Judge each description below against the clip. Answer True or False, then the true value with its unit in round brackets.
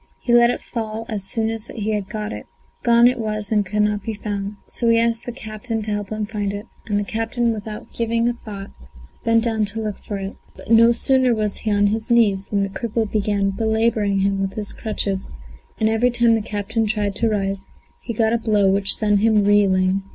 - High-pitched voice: True (215 Hz)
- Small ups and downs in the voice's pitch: True (2.0 semitones)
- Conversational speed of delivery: False (225 wpm)